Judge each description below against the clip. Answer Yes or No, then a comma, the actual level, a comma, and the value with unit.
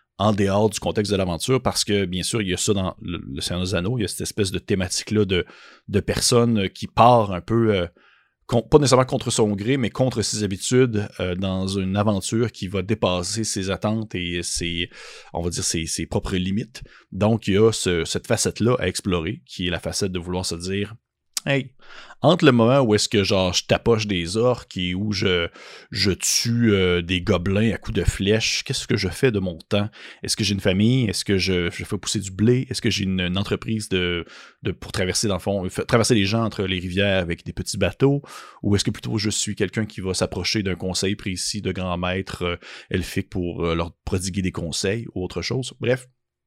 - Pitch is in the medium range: No, low, 100 Hz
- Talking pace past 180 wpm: Yes, fast, 220 wpm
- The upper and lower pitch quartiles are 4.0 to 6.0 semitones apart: No, average, 3.4 semitones